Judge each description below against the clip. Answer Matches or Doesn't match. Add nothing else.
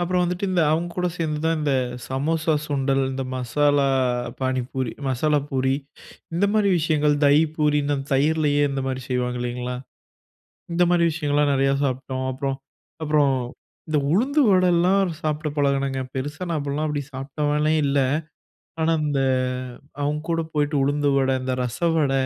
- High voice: Doesn't match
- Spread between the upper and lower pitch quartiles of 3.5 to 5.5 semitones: Doesn't match